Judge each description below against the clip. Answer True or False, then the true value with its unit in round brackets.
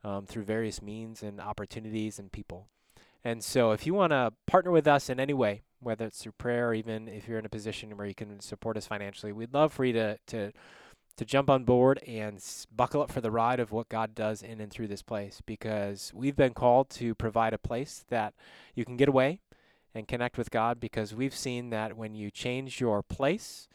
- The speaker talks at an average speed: False (225 wpm)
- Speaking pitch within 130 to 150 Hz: False (115 Hz)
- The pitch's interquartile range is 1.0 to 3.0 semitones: True (2.7 semitones)